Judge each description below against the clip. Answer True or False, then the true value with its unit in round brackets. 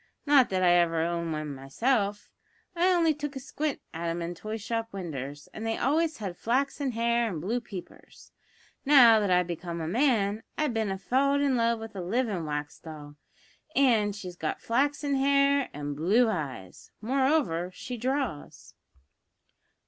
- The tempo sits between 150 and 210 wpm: True (165 wpm)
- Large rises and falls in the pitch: True (7.6 semitones)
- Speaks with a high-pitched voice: True (220 Hz)